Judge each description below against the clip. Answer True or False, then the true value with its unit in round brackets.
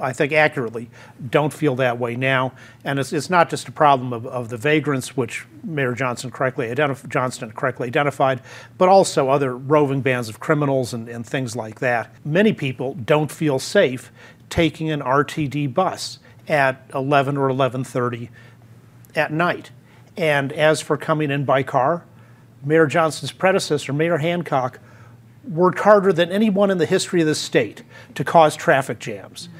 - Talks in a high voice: False (140 Hz)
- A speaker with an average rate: True (160 wpm)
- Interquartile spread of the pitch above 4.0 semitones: False (3.7 semitones)